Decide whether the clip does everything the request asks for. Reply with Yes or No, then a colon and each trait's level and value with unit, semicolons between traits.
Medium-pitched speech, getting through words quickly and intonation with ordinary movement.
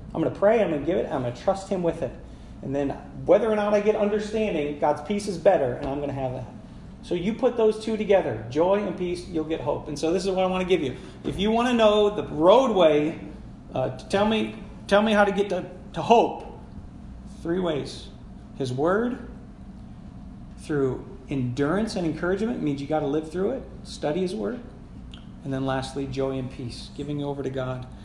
No: medium, 175 Hz; fast, 210 wpm; wide, 6.4 semitones